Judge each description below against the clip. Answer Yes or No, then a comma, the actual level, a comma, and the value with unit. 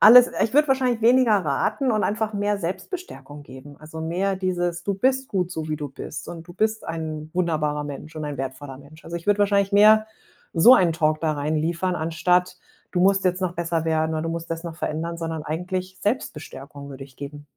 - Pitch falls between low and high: Yes, medium, 170 Hz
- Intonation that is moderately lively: Yes, average, 4.4 semitones